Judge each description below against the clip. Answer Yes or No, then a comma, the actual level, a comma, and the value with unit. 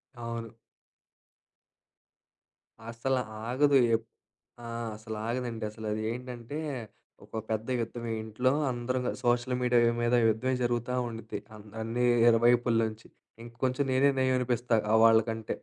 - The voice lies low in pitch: Yes, low, 120 Hz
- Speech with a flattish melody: Yes, narrow, 1.8 semitones